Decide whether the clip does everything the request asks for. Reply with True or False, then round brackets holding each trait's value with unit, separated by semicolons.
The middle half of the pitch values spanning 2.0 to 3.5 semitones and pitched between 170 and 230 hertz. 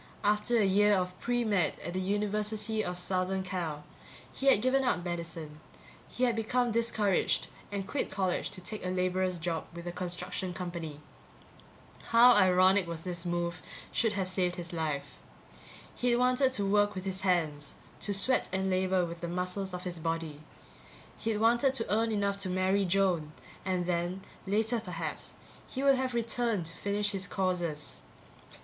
True (3.2 semitones; 190 Hz)